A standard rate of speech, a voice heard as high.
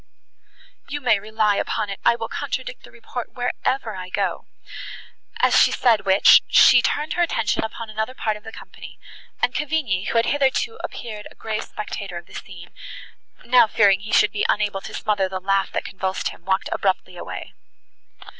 Yes: average, 180 wpm; high, 215 Hz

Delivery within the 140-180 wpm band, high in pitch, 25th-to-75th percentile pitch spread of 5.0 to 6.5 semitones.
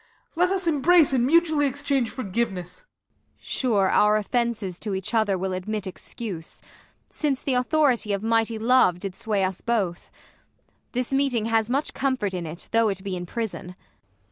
Yes: average, 170 wpm; high, 225 Hz; wide, 5.4 semitones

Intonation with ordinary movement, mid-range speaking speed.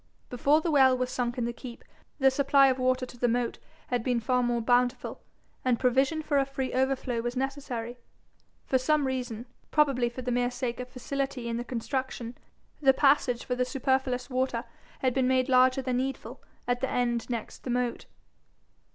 No: narrow, 1.5 semitones; average, 185 wpm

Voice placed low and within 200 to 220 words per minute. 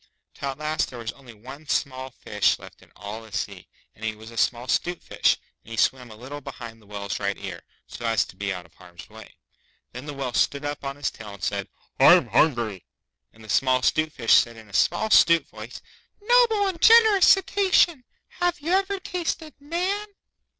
Yes: low, 130 Hz; fast, 205 wpm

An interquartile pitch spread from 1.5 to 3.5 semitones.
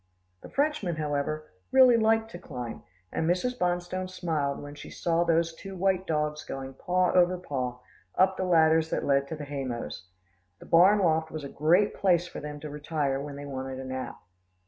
No: average, 4.2 semitones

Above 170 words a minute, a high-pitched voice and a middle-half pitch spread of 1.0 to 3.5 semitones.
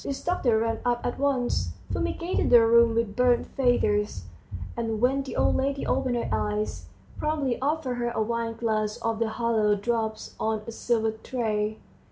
No: average, 165 wpm; high, 230 Hz; narrow, 2.4 semitones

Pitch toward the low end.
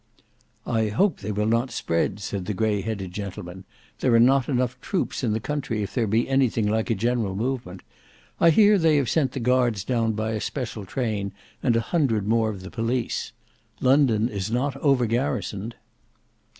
Yes: low, 115 Hz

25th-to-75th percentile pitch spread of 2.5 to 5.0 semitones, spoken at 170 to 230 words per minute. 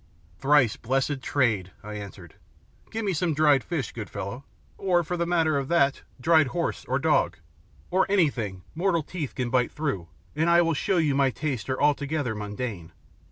No: wide, 5.5 semitones; average, 175 wpm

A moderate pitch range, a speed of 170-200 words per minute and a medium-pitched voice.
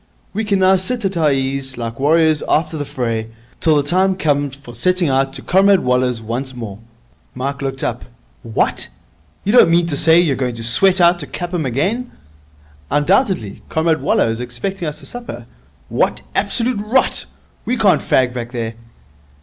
No: wide, 6.8 semitones; average, 175 wpm; medium, 150 Hz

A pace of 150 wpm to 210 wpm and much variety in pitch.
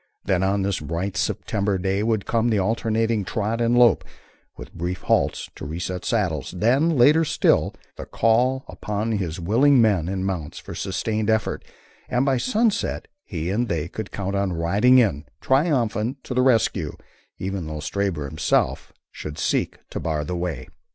No: average, 165 wpm; average, 4.7 semitones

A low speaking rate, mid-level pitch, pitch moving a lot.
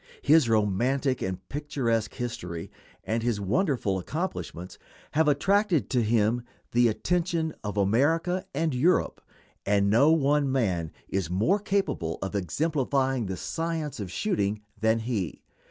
No: slow, 130 wpm; low, 120 Hz; wide, 7.3 semitones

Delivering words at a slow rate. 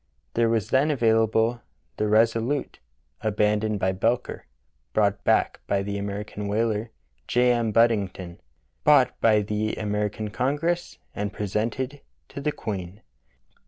Yes: slow, 125 wpm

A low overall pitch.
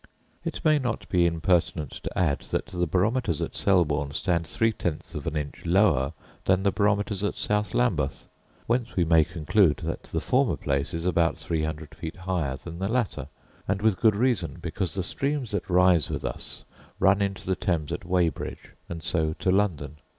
Yes: very low, 90 Hz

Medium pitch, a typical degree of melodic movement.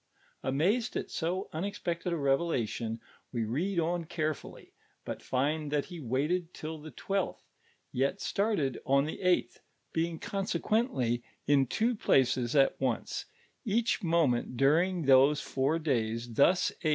Yes: medium, 155 Hz; average, 5.0 semitones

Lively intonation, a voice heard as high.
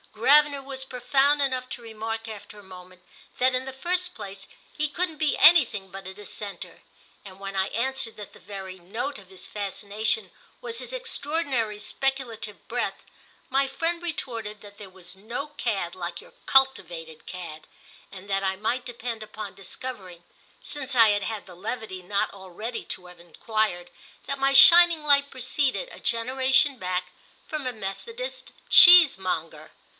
Yes: wide, 6.0 semitones; high, 225 Hz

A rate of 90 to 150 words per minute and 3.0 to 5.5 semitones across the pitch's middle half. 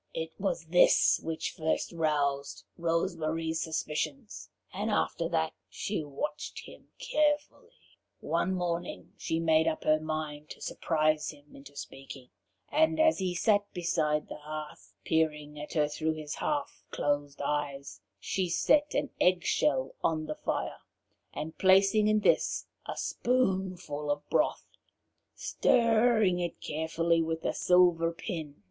Yes: average, 140 wpm; average, 3.7 semitones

